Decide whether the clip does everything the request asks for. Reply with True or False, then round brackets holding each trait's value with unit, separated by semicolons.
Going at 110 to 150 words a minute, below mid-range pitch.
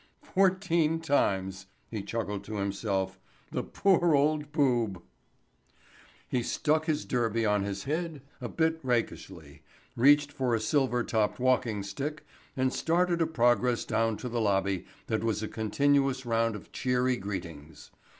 True (140 wpm; 120 Hz)